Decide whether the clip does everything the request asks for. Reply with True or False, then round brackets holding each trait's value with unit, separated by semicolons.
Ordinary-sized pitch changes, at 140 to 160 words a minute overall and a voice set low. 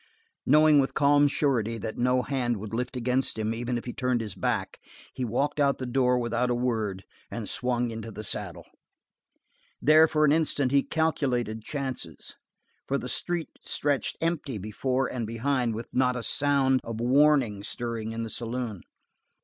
False (3.4 semitones; 170 wpm; 125 Hz)